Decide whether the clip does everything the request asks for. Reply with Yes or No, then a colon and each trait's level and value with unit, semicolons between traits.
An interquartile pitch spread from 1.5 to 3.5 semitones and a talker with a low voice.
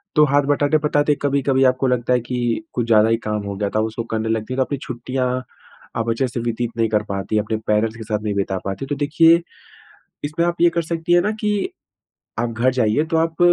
No: average, 4.9 semitones; low, 125 Hz